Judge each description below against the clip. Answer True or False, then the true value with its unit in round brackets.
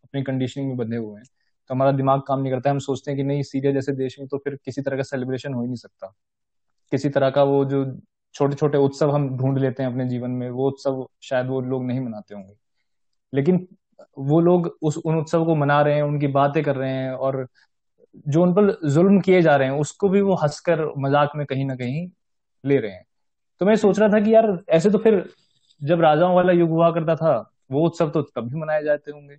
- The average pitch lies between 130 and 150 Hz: True (140 Hz)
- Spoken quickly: True (235 wpm)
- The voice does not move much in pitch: False (3.6 semitones)